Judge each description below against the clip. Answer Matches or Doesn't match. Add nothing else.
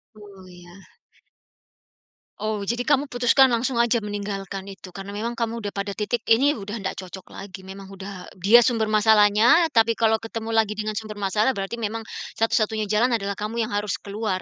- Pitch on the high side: Matches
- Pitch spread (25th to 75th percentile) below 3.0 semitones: Matches